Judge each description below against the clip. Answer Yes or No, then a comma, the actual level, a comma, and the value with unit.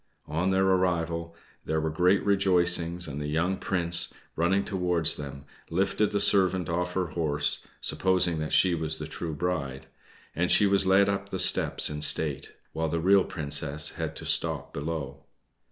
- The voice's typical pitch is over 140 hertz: No, very low, 85 Hz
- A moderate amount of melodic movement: Yes, average, 3.3 semitones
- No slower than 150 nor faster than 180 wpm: Yes, average, 170 wpm